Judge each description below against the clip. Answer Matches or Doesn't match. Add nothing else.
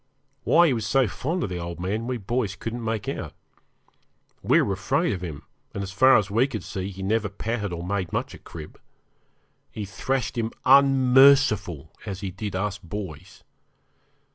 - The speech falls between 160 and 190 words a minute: Matches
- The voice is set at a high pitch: Doesn't match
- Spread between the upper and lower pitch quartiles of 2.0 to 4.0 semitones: Doesn't match